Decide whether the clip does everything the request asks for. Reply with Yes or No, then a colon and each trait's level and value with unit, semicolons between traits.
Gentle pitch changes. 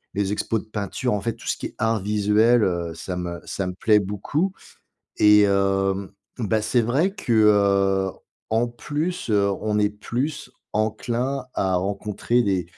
No: average, 3.2 semitones